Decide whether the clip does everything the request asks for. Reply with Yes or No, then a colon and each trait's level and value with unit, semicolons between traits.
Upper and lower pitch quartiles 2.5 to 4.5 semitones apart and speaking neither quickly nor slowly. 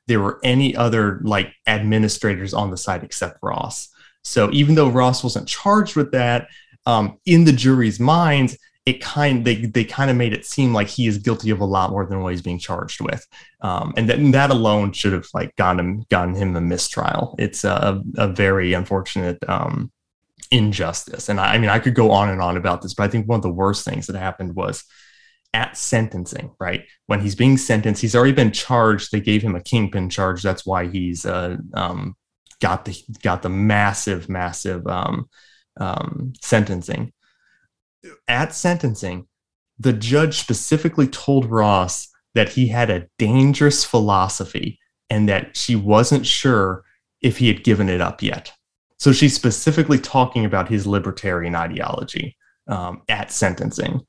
No: average, 4.9 semitones; average, 180 wpm